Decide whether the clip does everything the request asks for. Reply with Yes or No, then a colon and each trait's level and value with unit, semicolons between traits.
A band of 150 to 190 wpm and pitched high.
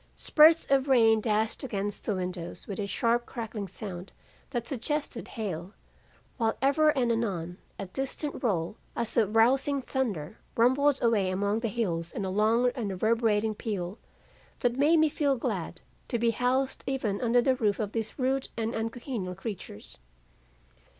Yes: average, 155 wpm; high, 225 Hz